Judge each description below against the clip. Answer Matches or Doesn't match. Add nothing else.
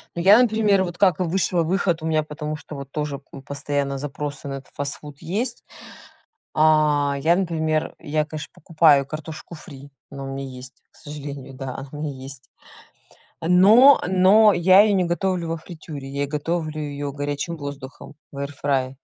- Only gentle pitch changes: Doesn't match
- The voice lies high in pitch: Doesn't match